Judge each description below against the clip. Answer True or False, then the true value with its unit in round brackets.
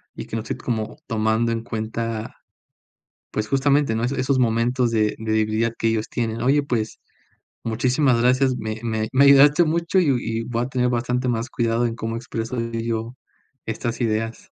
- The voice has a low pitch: True (115 Hz)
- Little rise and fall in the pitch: True (2.2 semitones)